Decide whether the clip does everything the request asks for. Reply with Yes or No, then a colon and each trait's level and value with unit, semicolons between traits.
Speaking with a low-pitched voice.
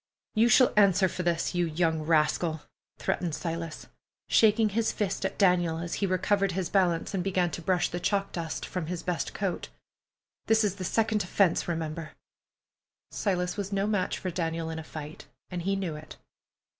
No: medium, 180 Hz